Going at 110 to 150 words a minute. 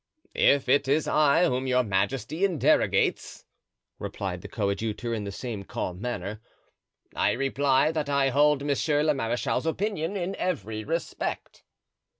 Yes: average, 140 wpm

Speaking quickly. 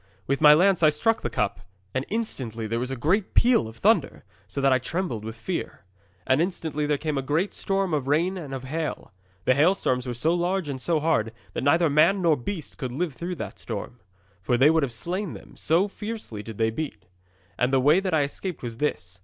Yes: fast, 220 wpm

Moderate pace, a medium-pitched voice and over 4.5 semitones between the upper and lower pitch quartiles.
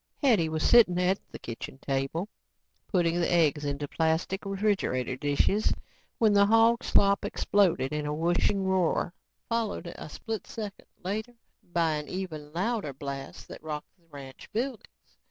Yes: average, 150 wpm; medium, 175 Hz; wide, 5.4 semitones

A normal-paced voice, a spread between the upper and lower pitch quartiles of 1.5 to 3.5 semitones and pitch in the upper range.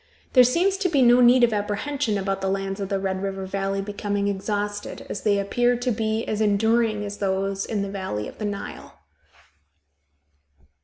Yes: average, 185 wpm; average, 2.9 semitones; high, 205 Hz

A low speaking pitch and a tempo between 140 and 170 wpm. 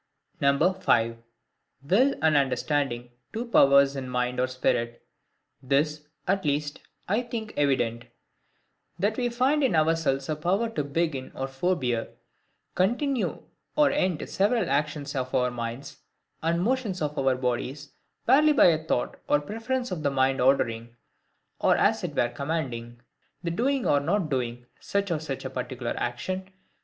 No: medium, 150 Hz; average, 145 wpm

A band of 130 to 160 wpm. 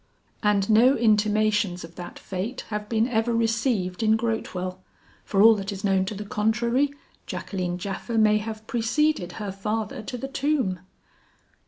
Yes: average, 155 wpm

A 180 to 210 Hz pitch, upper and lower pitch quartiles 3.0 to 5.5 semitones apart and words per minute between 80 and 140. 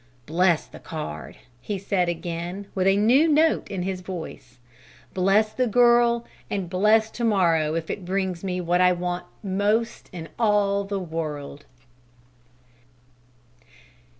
Yes: high, 190 Hz; average, 3.3 semitones; slow, 135 wpm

